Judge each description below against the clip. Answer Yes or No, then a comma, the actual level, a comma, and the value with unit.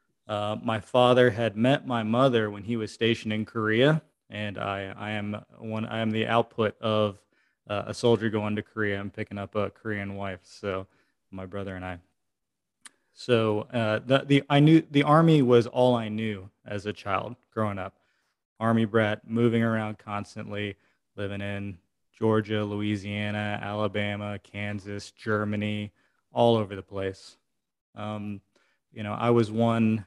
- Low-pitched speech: Yes, low, 105 Hz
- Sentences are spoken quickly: No, average, 160 wpm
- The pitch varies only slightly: Yes, narrow, 2.0 semitones